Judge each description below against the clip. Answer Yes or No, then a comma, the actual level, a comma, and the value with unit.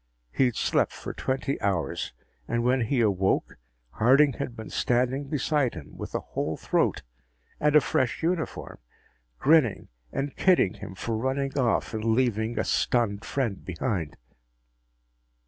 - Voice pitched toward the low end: Yes, low, 120 Hz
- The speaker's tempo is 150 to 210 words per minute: No, average, 140 wpm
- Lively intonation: No, average, 4.1 semitones